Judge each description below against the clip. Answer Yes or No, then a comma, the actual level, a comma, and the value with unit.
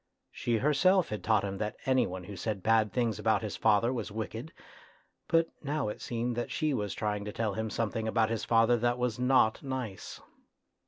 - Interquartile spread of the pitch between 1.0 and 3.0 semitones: Yes, average, 2.7 semitones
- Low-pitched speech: Yes, low, 115 Hz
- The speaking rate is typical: Yes, average, 195 wpm